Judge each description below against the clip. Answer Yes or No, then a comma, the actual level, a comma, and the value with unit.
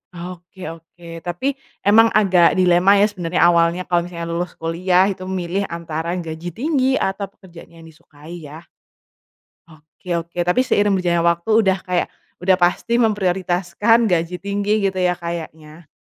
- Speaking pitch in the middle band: Yes, medium, 180 Hz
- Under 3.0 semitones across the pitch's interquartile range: Yes, narrow, 2.5 semitones